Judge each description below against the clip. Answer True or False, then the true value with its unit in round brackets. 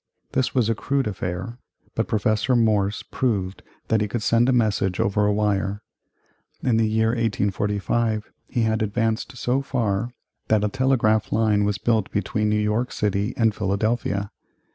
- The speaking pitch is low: True (110 Hz)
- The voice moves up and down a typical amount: False (2.3 semitones)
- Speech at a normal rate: True (160 wpm)